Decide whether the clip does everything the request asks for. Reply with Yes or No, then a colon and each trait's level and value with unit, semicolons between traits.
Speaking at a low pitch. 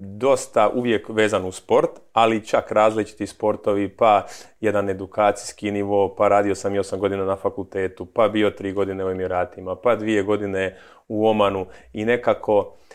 Yes: low, 100 Hz